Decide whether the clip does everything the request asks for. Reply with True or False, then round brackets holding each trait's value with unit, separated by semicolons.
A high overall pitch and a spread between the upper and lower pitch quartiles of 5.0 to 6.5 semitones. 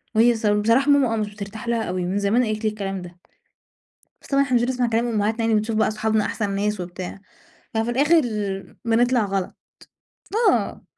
False (220 Hz; 2.8 semitones)